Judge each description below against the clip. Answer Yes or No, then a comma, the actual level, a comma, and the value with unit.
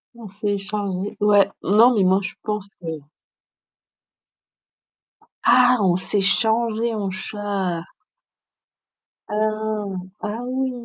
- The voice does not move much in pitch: Yes, narrow, 2.1 semitones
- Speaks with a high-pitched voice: Yes, high, 210 Hz